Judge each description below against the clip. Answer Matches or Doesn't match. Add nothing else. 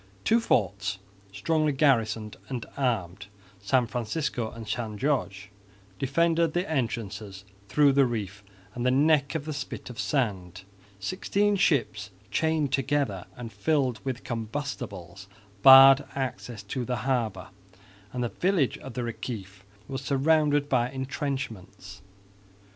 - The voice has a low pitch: Matches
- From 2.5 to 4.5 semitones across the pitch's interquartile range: Doesn't match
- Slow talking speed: Matches